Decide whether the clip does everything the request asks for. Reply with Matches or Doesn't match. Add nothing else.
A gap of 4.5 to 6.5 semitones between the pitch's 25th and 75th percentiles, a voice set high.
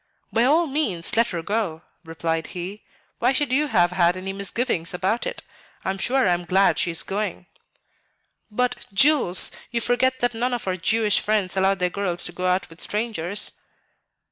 Matches